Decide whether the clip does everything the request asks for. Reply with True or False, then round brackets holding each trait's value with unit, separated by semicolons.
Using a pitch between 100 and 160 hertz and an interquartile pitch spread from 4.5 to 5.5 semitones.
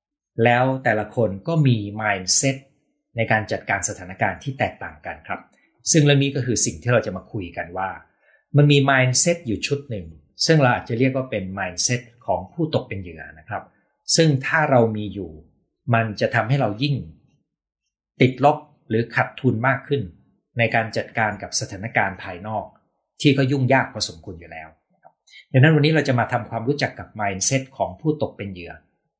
True (120 Hz; 5.1 semitones)